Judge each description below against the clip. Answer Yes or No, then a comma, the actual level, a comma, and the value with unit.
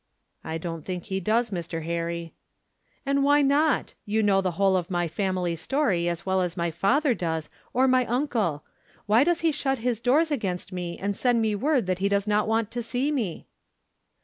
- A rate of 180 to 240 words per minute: Yes, average, 200 wpm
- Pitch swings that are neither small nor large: No, wide, 6.4 semitones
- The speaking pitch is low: No, high, 205 Hz